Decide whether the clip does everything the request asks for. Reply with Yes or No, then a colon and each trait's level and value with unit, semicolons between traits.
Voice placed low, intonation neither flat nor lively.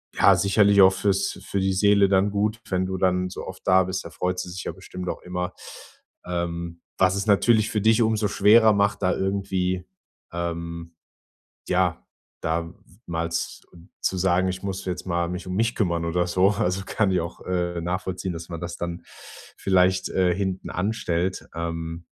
No: very low, 90 Hz; narrow, 2.2 semitones